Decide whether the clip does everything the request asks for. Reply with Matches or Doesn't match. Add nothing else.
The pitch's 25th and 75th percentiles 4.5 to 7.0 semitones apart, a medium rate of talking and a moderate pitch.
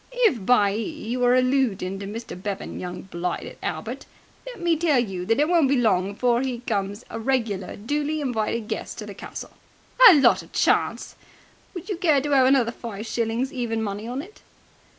Doesn't match